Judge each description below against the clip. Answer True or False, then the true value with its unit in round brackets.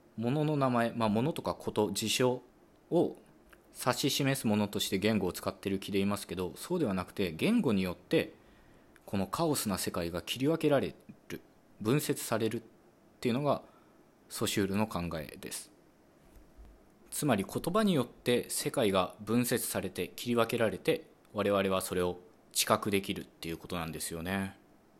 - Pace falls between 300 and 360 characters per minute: True (320 characters per minute)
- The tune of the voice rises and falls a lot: False (4.5 semitones)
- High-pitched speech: False (105 Hz)